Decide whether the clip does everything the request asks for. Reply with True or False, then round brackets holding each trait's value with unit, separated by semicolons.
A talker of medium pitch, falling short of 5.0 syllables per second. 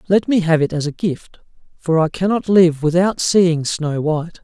True (170 Hz; 4.8 syllables/s)